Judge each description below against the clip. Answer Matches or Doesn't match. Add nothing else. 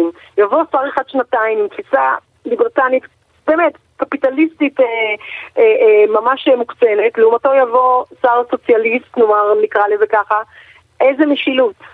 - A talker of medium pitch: Doesn't match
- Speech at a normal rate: Matches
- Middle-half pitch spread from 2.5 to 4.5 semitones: Doesn't match